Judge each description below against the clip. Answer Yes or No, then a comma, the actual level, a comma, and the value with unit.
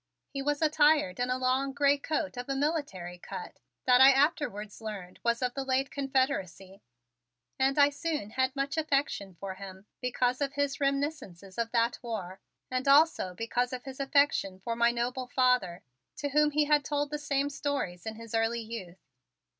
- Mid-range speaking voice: No, very high, 260 Hz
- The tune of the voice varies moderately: Yes, average, 4.2 semitones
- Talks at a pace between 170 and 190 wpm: Yes, average, 180 wpm